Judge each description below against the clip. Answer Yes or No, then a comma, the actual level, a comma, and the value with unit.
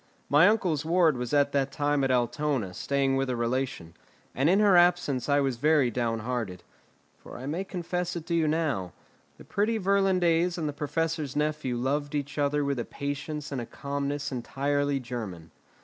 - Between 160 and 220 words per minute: Yes, average, 180 wpm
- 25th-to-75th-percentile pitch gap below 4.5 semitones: Yes, average, 4.0 semitones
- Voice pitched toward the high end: No, medium, 145 Hz